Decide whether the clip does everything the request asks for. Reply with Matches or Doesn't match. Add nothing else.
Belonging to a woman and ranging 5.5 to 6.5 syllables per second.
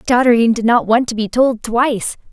Matches